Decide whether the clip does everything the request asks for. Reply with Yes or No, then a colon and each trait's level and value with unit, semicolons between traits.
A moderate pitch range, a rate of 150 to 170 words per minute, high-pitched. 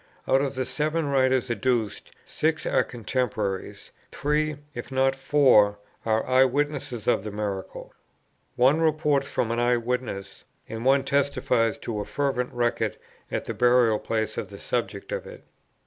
No: average, 3.6 semitones; average, 155 wpm; low, 125 Hz